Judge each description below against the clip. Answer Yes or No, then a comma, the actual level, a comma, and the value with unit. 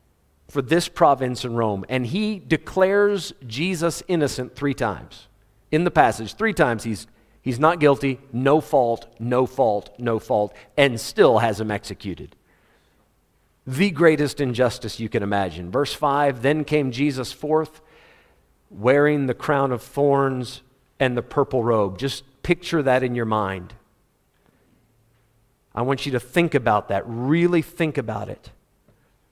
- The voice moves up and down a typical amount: Yes, average, 4.6 semitones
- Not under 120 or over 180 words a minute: Yes, average, 145 wpm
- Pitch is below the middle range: Yes, low, 130 Hz